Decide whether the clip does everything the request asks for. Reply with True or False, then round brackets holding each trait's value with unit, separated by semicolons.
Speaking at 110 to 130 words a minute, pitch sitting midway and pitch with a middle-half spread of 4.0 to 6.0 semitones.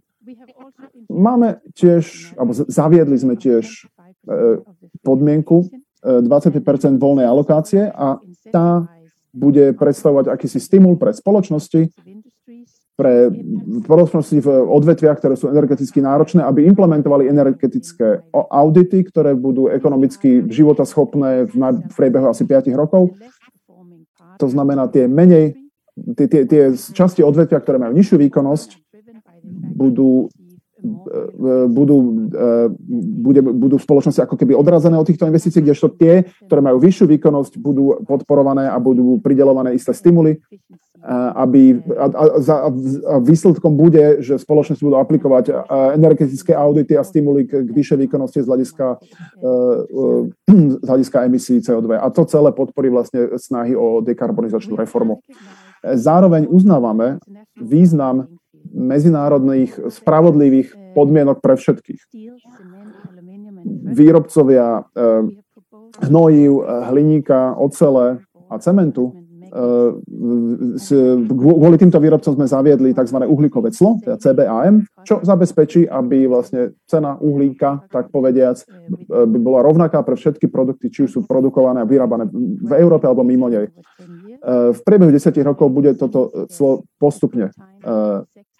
True (115 wpm; 150 Hz; 5.5 semitones)